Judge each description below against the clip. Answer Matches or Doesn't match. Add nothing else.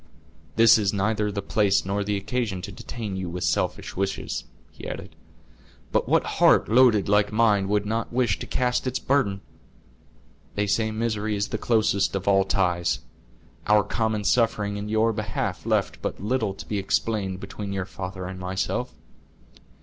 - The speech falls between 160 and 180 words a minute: Matches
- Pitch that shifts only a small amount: Matches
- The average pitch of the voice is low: Matches